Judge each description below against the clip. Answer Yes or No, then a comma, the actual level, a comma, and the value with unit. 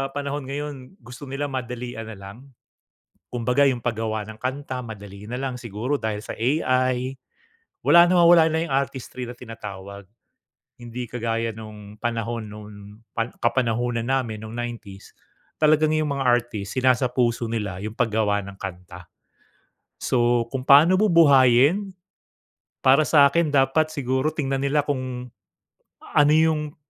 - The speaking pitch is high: No, low, 125 Hz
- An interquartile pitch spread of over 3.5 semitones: Yes, average, 3.9 semitones